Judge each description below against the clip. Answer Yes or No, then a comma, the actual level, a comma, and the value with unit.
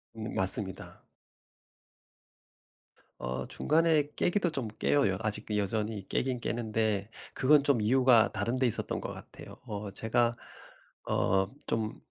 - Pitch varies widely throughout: No, average, 3.9 semitones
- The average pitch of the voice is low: Yes, low, 110 Hz